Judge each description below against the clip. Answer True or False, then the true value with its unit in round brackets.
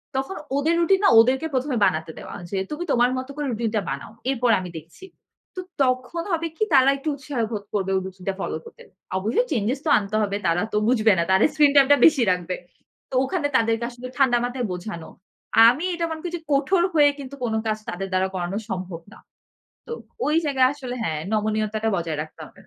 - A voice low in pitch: False (240 Hz)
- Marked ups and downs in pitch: True (6.5 semitones)